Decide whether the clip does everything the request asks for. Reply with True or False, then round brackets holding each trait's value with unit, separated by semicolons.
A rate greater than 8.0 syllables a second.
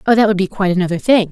True (8.6 syllables/s)